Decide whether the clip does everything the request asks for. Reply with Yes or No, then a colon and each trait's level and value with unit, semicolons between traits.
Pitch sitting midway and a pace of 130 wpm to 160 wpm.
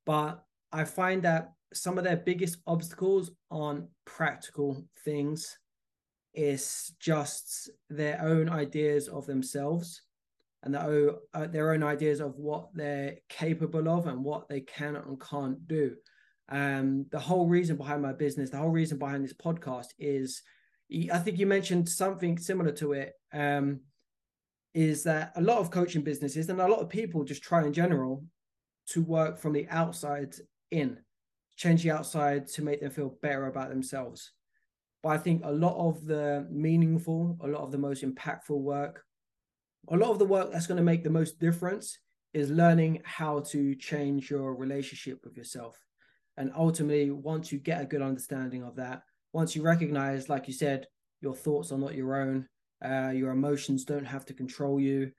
No: medium, 150 Hz; average, 170 wpm